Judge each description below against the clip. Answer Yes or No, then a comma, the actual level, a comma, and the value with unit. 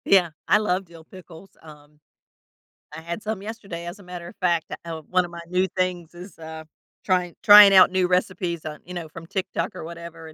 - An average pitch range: No, narrow, 2.1 semitones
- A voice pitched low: No, medium, 175 Hz